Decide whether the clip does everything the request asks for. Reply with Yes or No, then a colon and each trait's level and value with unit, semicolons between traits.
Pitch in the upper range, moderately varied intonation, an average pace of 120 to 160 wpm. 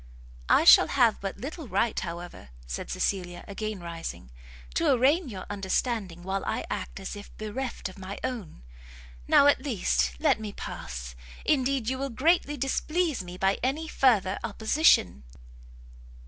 No: high, 210 Hz; wide, 6.9 semitones; average, 145 wpm